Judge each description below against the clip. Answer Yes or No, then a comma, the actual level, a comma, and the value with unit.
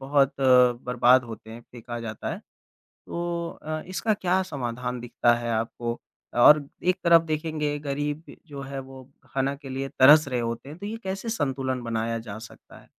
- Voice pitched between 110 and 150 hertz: Yes, low, 135 Hz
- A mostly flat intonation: No, average, 4.6 semitones